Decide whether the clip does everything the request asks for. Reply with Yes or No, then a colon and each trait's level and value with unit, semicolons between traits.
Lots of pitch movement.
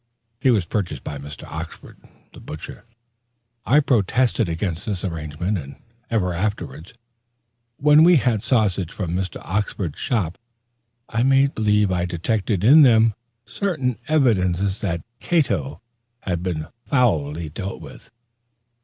Yes: wide, 5.9 semitones